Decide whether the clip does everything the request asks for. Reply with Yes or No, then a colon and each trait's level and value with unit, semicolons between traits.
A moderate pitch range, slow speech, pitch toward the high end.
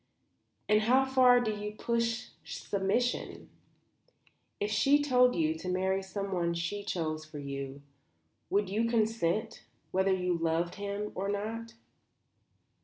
Yes: average, 4.5 semitones; slow, 125 wpm; high, 205 Hz